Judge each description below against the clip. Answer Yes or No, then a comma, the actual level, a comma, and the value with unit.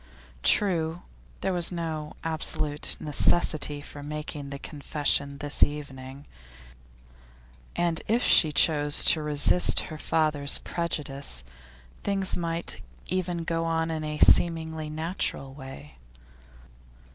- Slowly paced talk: Yes, slow, 110 wpm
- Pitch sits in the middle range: Yes, medium, 155 Hz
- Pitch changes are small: Yes, narrow, 2.3 semitones